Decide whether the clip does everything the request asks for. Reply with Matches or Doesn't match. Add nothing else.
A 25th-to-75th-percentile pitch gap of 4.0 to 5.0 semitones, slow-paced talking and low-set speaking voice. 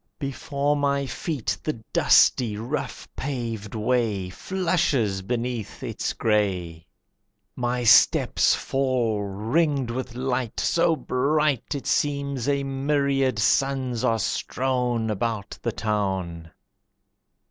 Matches